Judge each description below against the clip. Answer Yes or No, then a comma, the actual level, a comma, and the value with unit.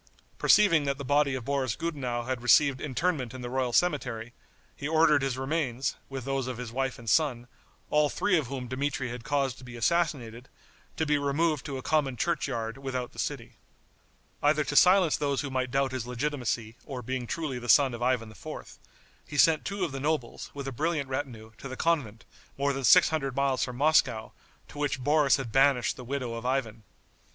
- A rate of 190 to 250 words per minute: Yes, average, 200 wpm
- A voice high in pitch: No, low, 135 Hz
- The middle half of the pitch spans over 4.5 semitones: No, average, 3.1 semitones